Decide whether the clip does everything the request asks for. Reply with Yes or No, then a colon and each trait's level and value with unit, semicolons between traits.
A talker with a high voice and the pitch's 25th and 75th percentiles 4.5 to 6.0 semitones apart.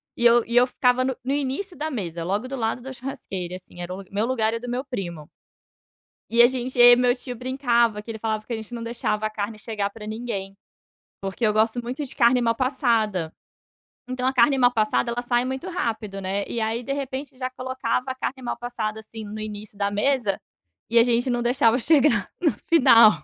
No: high, 235 Hz; average, 3.1 semitones